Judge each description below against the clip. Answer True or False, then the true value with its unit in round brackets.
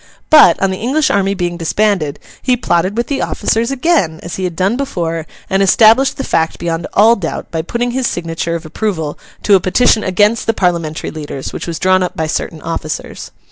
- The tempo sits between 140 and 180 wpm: False (200 wpm)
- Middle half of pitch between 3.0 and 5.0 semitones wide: False (5.6 semitones)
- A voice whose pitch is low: False (185 Hz)